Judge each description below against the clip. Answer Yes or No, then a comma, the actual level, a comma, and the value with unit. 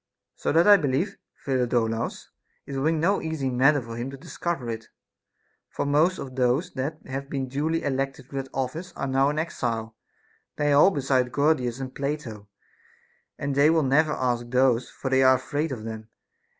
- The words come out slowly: No, average, 180 wpm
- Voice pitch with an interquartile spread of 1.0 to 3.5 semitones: Yes, average, 3.1 semitones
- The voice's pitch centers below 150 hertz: Yes, low, 135 Hz